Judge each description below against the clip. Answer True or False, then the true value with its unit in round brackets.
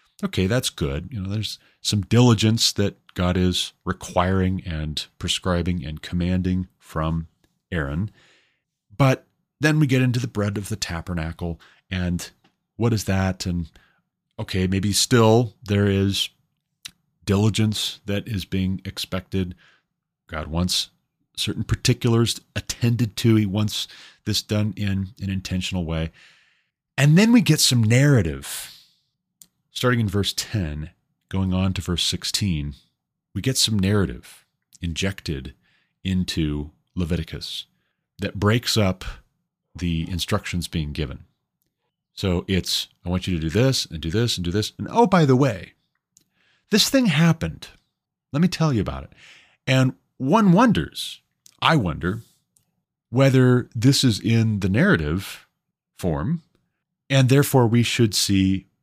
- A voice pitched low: True (100 Hz)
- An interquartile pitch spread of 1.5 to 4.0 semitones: False (5.6 semitones)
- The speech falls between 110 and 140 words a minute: True (135 wpm)